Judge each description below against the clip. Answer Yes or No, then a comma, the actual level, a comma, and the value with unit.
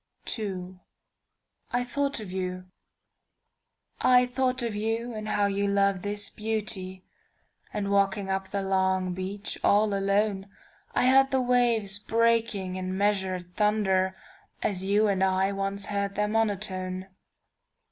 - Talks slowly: Yes, slow, 115 wpm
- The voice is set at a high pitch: Yes, high, 200 Hz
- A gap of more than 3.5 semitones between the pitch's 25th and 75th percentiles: No, narrow, 2.5 semitones